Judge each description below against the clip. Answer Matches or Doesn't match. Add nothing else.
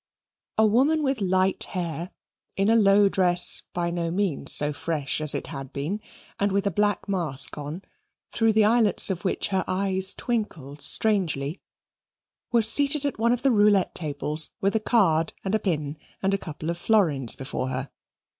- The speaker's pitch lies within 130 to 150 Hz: Doesn't match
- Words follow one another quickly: Doesn't match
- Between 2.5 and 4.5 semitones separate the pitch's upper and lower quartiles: Doesn't match